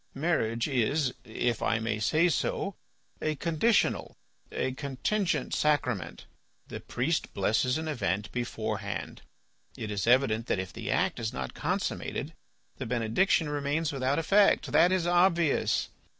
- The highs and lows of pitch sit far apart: Yes, wide, 6.4 semitones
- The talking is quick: No, slow, 135 wpm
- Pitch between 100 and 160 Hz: Yes, low, 135 Hz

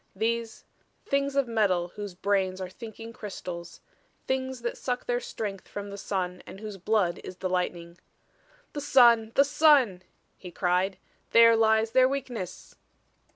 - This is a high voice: Yes, high, 220 Hz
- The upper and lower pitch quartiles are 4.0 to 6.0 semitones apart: Yes, average, 4.7 semitones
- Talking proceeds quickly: No, average, 150 wpm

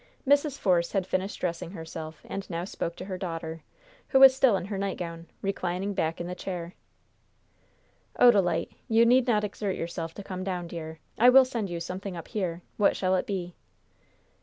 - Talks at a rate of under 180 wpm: No, average, 185 wpm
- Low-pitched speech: No, medium, 185 Hz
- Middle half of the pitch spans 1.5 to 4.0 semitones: Yes, average, 3.3 semitones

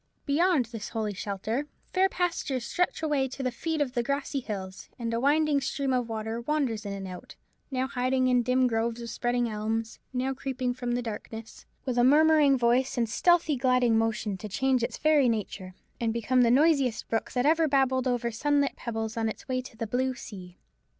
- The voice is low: No, very high, 250 Hz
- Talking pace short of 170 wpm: No, average, 195 wpm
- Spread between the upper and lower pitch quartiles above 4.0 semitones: No, average, 3.3 semitones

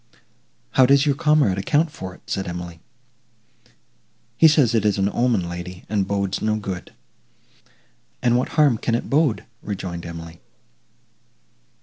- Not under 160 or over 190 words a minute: No, average, 140 wpm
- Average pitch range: No, wide, 6.2 semitones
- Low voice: Yes, low, 105 Hz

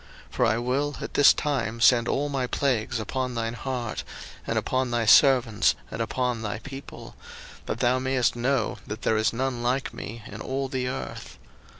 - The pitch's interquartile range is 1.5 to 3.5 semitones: Yes, narrow, 2.6 semitones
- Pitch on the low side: Yes, low, 125 Hz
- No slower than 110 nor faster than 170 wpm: No, average, 185 wpm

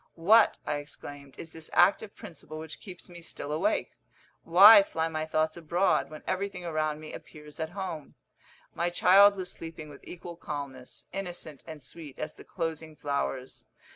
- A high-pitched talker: No, medium, 160 Hz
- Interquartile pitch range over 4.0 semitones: No, average, 2.8 semitones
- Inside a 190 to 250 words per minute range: No, average, 165 wpm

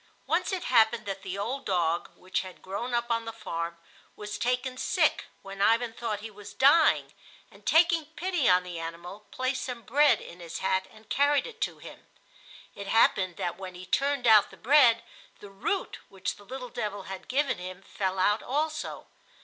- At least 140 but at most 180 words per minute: No, average, 190 wpm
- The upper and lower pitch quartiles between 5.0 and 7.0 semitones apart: Yes, average, 5.3 semitones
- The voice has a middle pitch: No, high, 215 Hz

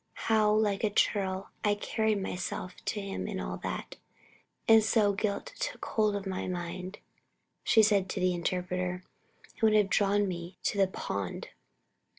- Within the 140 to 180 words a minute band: Yes, average, 160 wpm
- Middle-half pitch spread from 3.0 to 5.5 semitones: No, narrow, 2.5 semitones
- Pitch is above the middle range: Yes, high, 200 Hz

